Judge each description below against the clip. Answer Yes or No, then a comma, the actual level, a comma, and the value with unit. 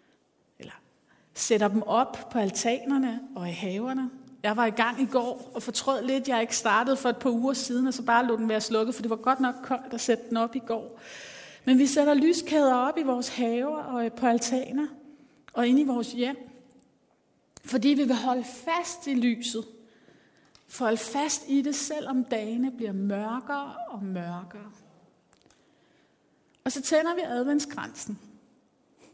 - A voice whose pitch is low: No, very high, 250 Hz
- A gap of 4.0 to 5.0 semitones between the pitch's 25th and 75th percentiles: No, average, 2.7 semitones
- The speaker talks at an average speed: Yes, average, 175 wpm